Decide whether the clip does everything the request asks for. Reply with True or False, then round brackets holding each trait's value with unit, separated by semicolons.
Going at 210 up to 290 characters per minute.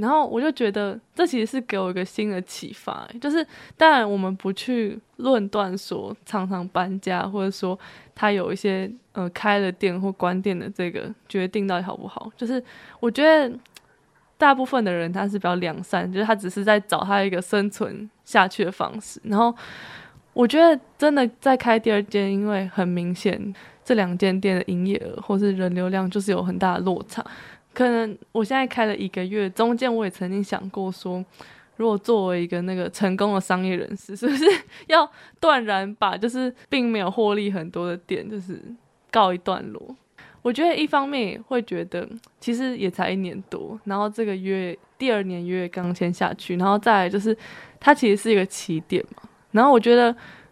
True (280 characters per minute)